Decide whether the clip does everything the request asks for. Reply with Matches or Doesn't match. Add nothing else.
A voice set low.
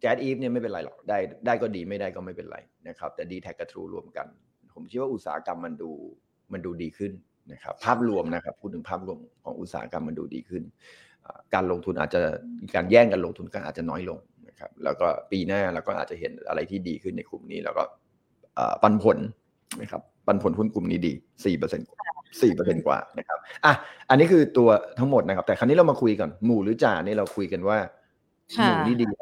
Matches